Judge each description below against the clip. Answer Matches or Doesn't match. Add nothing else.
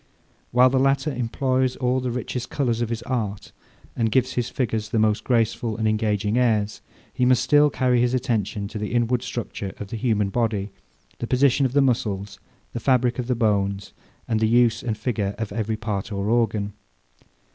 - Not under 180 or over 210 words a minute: Matches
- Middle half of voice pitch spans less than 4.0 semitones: Matches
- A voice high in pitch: Doesn't match